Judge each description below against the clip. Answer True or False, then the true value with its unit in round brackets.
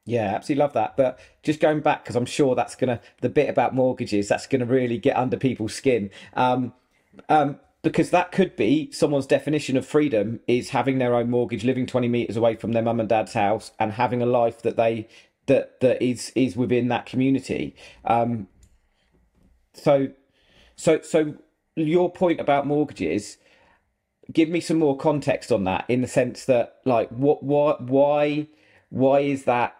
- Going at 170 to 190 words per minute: True (175 wpm)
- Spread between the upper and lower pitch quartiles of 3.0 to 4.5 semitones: True (3.7 semitones)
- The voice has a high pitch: False (130 Hz)